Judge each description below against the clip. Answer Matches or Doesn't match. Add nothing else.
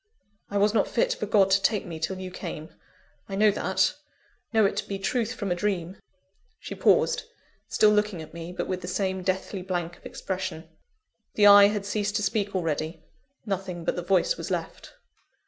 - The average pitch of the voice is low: Doesn't match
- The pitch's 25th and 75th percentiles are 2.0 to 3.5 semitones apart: Matches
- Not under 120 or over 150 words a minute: Doesn't match